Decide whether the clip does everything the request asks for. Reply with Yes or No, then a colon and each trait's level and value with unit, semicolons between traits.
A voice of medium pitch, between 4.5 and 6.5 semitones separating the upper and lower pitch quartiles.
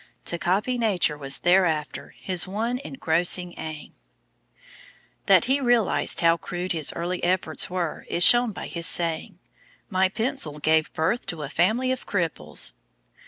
Yes: medium, 180 Hz; average, 5.1 semitones